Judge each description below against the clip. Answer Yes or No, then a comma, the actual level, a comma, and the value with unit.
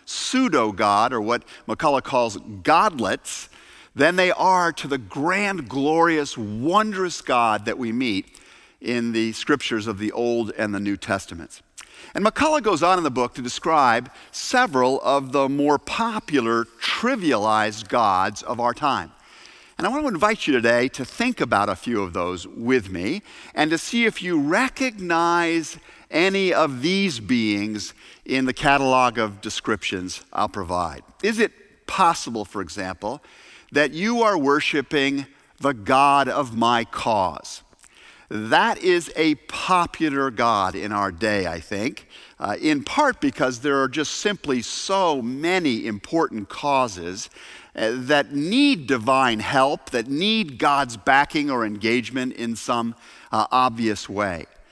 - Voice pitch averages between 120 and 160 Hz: Yes, medium, 140 Hz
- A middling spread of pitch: No, wide, 7.8 semitones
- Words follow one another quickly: No, average, 145 wpm